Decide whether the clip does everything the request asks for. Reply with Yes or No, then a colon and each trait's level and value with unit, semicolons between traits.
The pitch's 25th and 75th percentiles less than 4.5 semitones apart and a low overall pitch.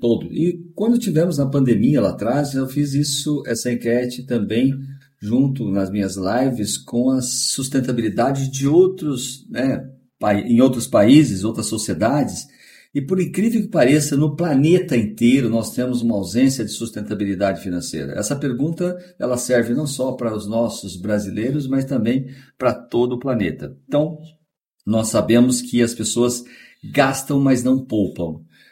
Yes: average, 3.8 semitones; low, 125 Hz